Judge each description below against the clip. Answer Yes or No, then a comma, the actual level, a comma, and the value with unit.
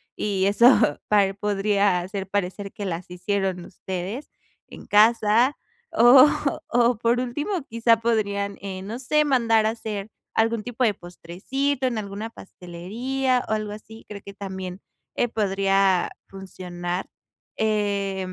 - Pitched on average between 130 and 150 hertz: No, high, 205 Hz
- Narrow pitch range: No, average, 3.2 semitones